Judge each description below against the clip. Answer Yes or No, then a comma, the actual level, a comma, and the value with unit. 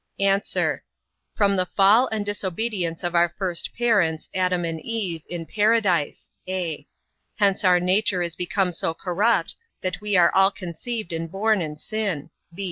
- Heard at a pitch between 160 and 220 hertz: Yes, medium, 185 Hz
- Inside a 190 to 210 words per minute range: No, average, 150 wpm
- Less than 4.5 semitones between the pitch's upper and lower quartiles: Yes, average, 3.3 semitones